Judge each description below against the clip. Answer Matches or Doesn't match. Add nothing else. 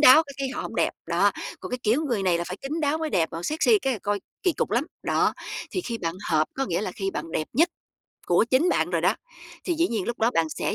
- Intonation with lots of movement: Matches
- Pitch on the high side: Matches